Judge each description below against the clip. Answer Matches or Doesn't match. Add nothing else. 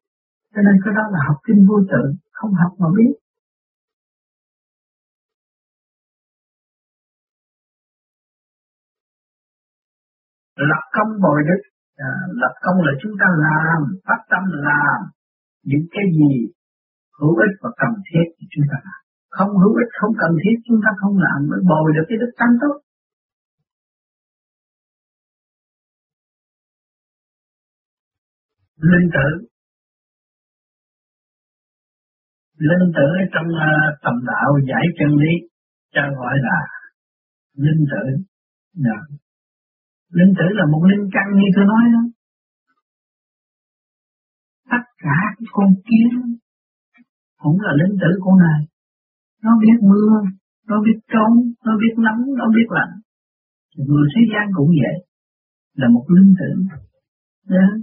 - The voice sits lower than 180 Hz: Doesn't match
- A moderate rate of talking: Doesn't match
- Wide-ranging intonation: Matches